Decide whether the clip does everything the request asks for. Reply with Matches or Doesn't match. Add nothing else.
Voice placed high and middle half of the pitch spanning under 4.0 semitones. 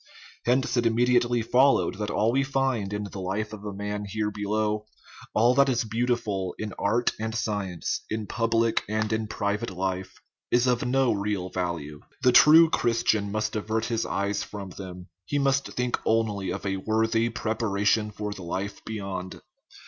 Doesn't match